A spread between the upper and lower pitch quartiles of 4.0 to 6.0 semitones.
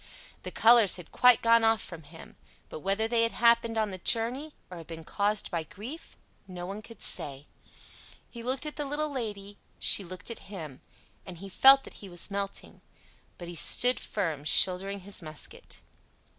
Yes: average, 4.7 semitones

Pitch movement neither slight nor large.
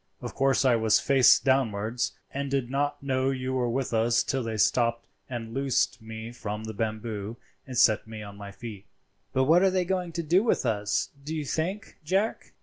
Yes: average, 3.9 semitones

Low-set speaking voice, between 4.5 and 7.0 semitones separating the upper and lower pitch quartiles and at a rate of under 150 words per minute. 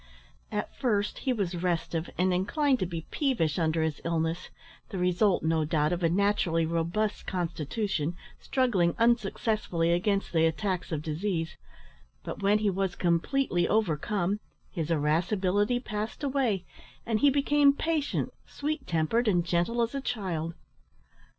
No: medium, 185 Hz; average, 4.8 semitones; average, 140 wpm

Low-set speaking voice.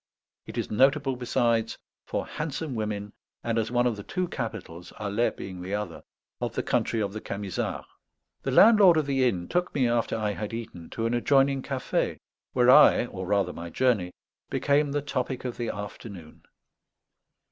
Yes: low, 115 Hz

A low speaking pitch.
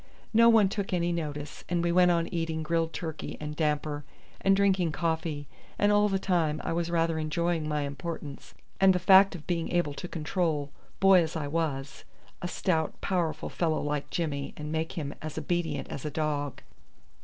No: medium, 165 Hz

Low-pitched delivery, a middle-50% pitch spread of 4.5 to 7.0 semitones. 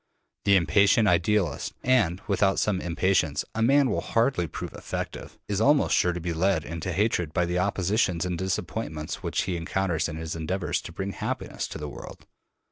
No: very low, 90 Hz; average, 3.4 semitones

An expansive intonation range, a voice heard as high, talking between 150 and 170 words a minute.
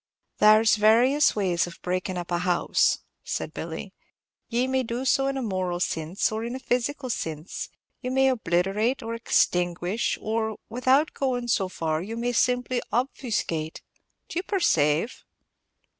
Yes: wide, 6.0 semitones; high, 225 Hz; average, 155 wpm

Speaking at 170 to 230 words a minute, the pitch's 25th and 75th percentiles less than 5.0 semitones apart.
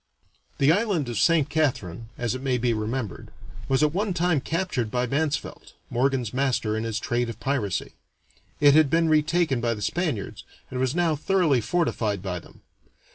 No: average, 175 wpm; average, 5.3 semitones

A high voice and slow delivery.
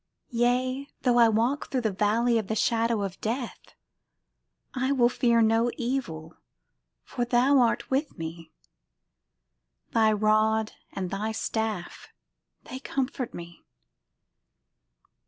Yes: high, 230 Hz; slow, 120 wpm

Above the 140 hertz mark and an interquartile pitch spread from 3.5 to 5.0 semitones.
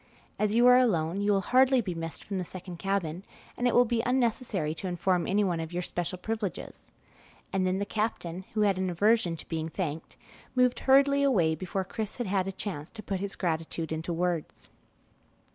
Yes: high, 190 Hz; average, 4.4 semitones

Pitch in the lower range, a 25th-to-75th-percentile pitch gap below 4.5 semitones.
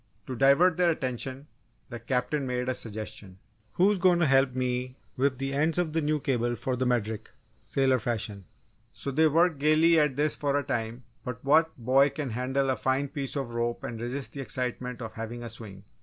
Yes: low, 130 Hz; average, 3.3 semitones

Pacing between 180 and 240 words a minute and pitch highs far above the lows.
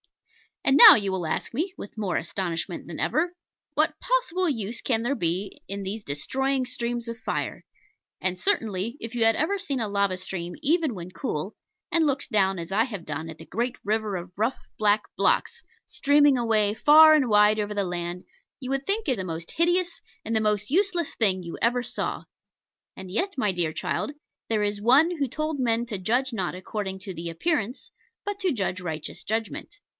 Yes: average, 195 wpm; wide, 6.4 semitones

